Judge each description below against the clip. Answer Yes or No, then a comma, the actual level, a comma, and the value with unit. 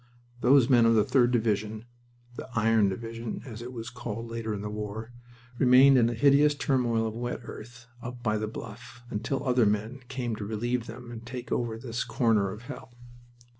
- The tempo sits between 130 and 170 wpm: No, average, 190 wpm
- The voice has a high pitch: No, low, 115 Hz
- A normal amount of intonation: No, narrow, 2.0 semitones